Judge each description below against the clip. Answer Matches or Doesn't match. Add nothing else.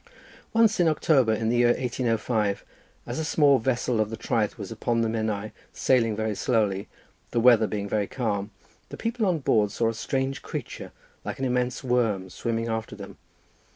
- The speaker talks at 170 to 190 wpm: Matches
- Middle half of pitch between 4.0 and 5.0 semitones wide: Doesn't match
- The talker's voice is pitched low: Matches